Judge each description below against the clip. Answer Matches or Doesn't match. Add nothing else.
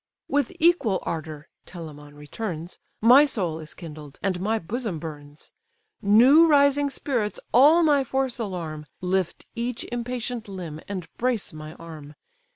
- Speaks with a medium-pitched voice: Doesn't match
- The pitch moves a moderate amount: Doesn't match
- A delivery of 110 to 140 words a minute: Matches